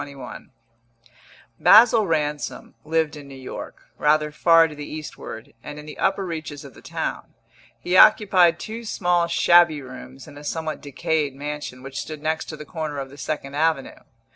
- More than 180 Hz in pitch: No, medium, 155 Hz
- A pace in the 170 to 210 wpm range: Yes, average, 180 wpm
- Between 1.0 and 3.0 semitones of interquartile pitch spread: Yes, average, 2.7 semitones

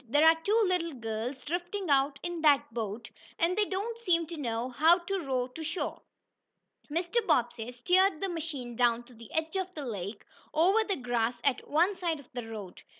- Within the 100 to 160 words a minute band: No, average, 195 wpm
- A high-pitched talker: Yes, very high, 305 Hz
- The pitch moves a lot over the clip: Yes, wide, 6.6 semitones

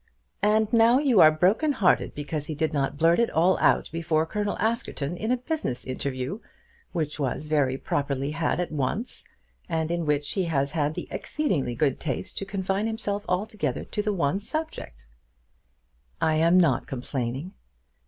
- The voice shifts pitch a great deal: Yes, wide, 6.2 semitones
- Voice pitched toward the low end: No, medium, 165 Hz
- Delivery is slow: No, average, 165 wpm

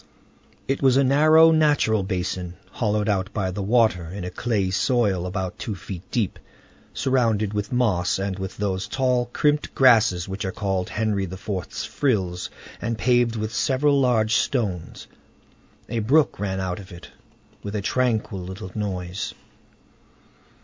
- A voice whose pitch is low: Yes, low, 105 Hz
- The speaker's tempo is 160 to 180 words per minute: No, average, 150 wpm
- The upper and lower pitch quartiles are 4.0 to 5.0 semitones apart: Yes, average, 4.5 semitones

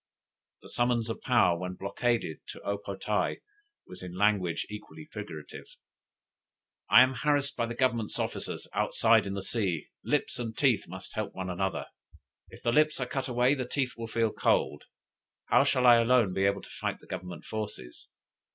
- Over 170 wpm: Yes, average, 180 wpm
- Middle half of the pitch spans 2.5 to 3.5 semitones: No, average, 4.3 semitones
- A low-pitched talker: Yes, low, 110 Hz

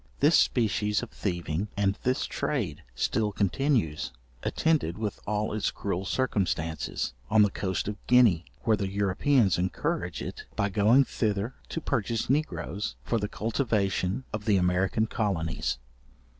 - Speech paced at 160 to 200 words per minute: No, average, 140 wpm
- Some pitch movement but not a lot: Yes, average, 3.7 semitones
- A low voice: Yes, low, 105 Hz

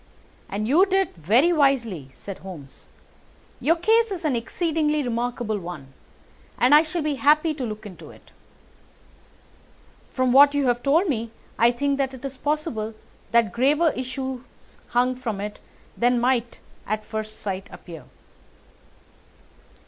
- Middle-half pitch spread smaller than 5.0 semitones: No, average, 5.3 semitones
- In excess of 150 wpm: No, average, 140 wpm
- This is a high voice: Yes, very high, 250 Hz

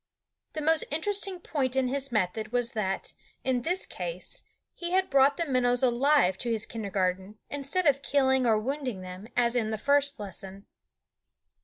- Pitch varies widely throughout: No, average, 5.0 semitones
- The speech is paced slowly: No, average, 165 wpm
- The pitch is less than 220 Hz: No, very high, 255 Hz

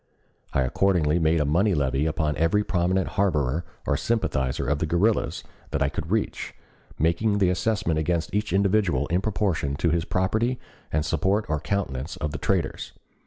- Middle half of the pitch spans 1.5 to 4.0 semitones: No, average, 4.9 semitones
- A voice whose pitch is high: No, very low, 85 Hz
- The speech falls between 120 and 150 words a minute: No, average, 165 wpm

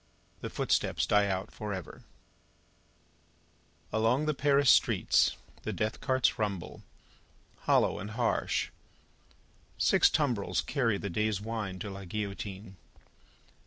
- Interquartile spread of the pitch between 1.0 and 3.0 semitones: No, average, 3.4 semitones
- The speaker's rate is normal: No, slow, 115 wpm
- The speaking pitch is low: Yes, low, 105 Hz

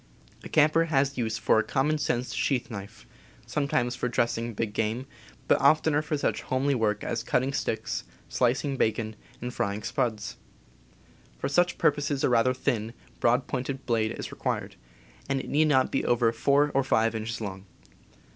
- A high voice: No, low, 125 Hz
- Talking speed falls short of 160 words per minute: No, average, 170 wpm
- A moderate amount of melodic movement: Yes, average, 3.6 semitones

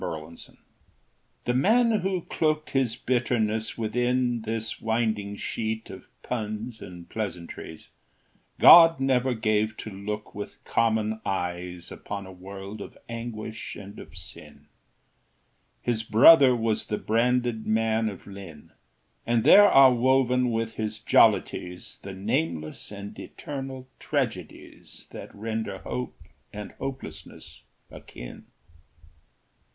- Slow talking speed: Yes, slow, 115 wpm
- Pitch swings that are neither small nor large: Yes, average, 3.6 semitones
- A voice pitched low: Yes, low, 110 Hz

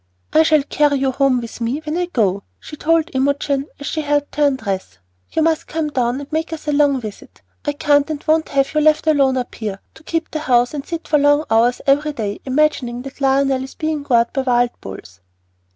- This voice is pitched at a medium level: No, very high, 280 Hz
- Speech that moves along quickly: Yes, fast, 220 wpm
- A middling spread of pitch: Yes, average, 3.5 semitones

